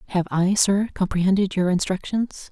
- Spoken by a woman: Yes, female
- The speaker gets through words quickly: No, average, 145 wpm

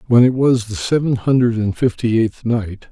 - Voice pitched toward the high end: No, low, 115 Hz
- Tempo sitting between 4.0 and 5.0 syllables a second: Yes, 4.8 syllables/s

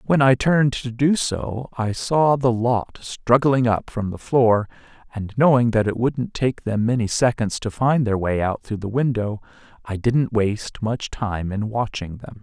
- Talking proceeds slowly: No, average, 195 wpm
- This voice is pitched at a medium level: No, low, 115 Hz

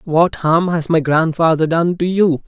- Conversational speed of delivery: Yes, average, 195 wpm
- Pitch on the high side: No, medium, 165 Hz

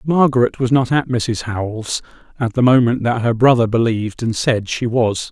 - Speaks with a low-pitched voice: Yes, low, 120 Hz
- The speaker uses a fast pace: No, average, 190 wpm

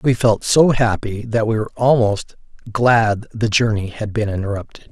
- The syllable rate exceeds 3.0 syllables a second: Yes, 4.7 syllables/s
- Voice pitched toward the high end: No, low, 110 Hz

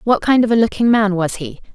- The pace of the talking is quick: Yes, fast, 275 wpm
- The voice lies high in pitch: Yes, high, 215 Hz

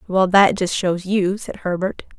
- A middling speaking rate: Yes, average, 190 wpm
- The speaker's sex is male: No, female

